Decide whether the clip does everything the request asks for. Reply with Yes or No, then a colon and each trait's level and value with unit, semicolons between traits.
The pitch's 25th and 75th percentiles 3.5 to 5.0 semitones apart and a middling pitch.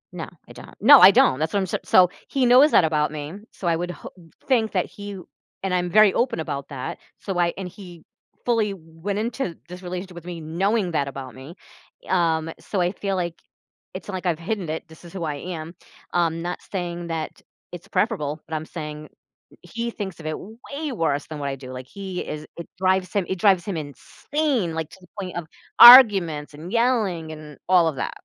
Yes: average, 3.9 semitones; medium, 175 Hz